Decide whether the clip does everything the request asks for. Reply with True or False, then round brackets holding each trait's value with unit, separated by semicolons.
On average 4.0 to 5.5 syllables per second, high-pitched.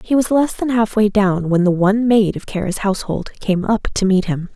True (5.4 syllables/s; 205 Hz)